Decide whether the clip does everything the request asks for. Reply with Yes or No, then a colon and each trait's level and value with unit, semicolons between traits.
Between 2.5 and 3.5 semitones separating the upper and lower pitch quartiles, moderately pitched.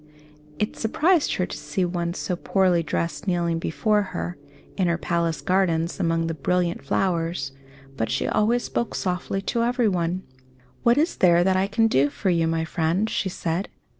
Yes: average, 3.1 semitones; medium, 180 Hz